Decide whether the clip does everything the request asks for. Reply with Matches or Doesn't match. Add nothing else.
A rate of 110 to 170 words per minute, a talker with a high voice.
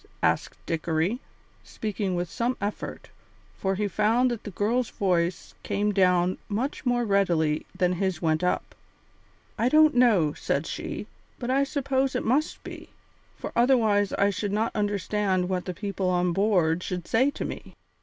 Matches